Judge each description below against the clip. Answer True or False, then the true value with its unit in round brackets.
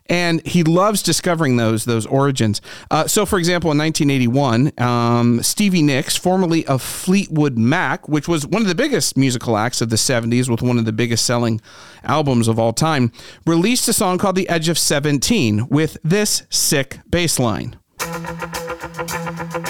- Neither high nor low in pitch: True (150 Hz)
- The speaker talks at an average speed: True (165 wpm)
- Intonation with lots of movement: True (6.1 semitones)